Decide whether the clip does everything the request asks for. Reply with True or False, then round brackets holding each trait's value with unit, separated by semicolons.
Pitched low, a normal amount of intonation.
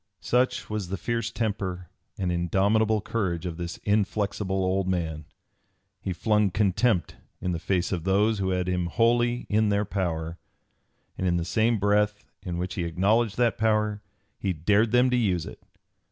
True (100 Hz; 3.4 semitones)